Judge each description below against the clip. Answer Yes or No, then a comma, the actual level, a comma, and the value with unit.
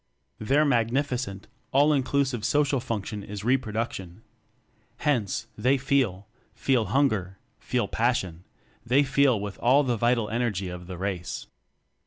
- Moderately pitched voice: No, low, 120 Hz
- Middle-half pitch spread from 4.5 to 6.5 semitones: Yes, average, 5.2 semitones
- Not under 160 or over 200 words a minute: No, slow, 135 wpm